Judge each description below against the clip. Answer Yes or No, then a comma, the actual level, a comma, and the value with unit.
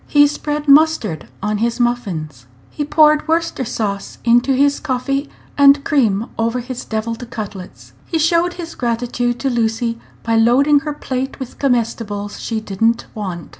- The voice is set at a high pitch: Yes, high, 240 Hz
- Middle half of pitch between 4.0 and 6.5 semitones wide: Yes, average, 4.4 semitones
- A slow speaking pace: No, average, 155 wpm